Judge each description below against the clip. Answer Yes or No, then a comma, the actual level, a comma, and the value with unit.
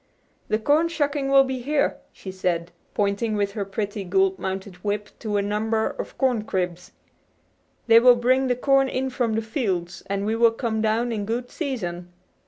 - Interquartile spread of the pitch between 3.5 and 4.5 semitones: Yes, average, 4.1 semitones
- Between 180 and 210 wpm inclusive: Yes, average, 185 wpm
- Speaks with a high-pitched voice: Yes, high, 220 Hz